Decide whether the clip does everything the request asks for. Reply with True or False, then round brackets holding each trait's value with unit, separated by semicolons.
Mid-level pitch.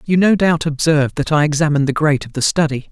True (150 Hz)